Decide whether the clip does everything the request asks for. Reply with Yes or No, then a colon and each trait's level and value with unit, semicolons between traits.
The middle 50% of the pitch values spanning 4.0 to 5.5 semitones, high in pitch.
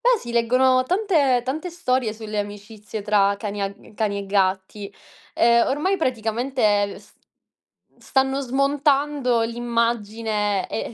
Yes: average, 4.3 semitones; high, 235 Hz